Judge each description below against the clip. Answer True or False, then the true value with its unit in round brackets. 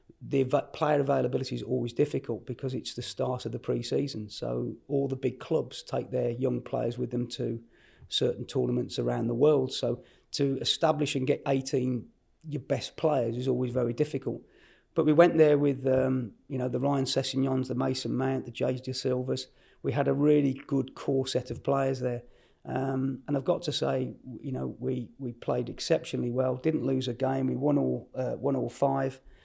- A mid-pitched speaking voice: False (130 Hz)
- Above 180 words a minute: True (190 wpm)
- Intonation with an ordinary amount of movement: False (2.0 semitones)